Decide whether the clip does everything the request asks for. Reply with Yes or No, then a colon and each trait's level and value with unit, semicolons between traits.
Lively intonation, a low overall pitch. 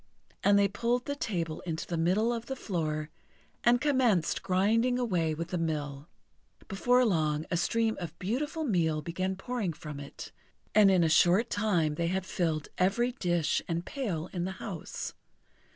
No: wide, 5.7 semitones; medium, 185 Hz